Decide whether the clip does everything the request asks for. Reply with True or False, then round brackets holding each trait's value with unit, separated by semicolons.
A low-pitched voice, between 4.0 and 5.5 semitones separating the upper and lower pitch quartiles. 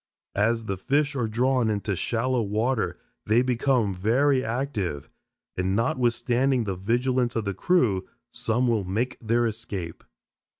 False (115 Hz; 3.6 semitones)